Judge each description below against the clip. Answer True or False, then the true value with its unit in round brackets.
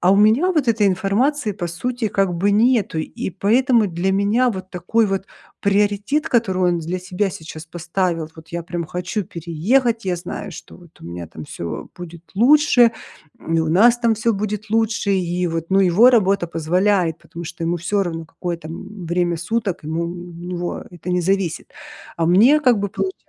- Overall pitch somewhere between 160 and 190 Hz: True (185 Hz)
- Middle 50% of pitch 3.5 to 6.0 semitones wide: True (4.1 semitones)